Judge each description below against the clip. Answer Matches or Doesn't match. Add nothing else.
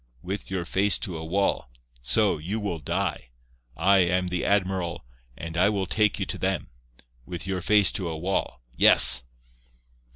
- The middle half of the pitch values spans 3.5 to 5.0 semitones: Doesn't match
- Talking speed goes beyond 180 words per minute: Doesn't match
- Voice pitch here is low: Matches